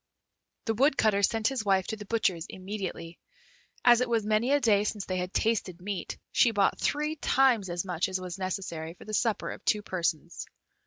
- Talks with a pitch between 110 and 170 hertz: No, high, 205 Hz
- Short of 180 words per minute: No, average, 195 wpm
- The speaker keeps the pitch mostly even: No, average, 3.6 semitones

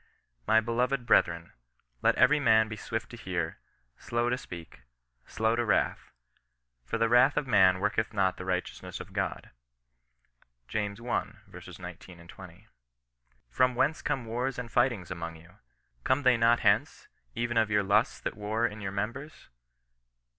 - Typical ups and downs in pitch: Yes, average, 4.4 semitones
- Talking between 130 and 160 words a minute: Yes, average, 155 wpm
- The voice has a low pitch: Yes, low, 110 Hz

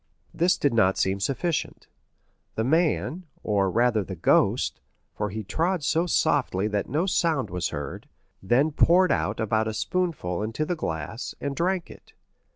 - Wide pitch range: Yes, wide, 8.5 semitones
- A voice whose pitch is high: No, low, 120 Hz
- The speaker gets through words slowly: No, average, 150 wpm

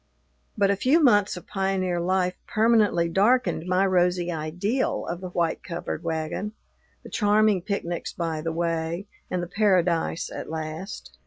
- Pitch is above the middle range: No, medium, 180 Hz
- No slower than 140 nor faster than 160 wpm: Yes, average, 150 wpm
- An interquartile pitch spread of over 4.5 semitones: No, average, 3.2 semitones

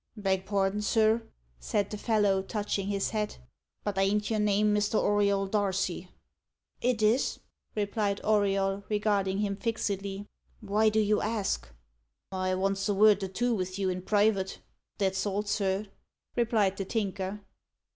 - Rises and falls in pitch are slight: Yes, narrow, 1.5 semitones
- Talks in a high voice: Yes, high, 205 Hz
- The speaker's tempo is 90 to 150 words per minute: Yes, average, 145 wpm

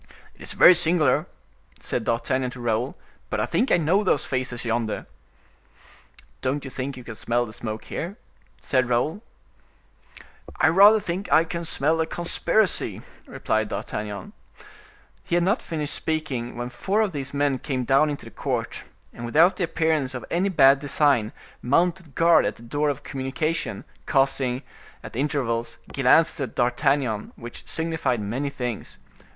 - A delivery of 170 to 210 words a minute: No, average, 155 wpm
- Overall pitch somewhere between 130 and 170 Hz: Yes, medium, 140 Hz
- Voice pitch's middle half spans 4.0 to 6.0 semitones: Yes, average, 4.8 semitones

